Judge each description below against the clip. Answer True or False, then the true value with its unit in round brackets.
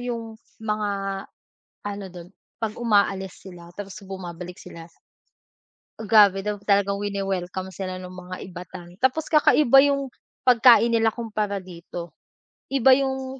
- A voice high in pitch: True (205 Hz)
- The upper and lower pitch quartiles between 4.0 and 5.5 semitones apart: True (4.3 semitones)